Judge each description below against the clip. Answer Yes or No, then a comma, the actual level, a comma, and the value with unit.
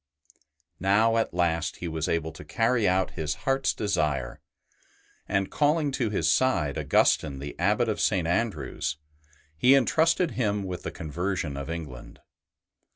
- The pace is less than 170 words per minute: Yes, average, 145 wpm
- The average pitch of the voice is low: Yes, very low, 95 Hz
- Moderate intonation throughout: No, wide, 6.6 semitones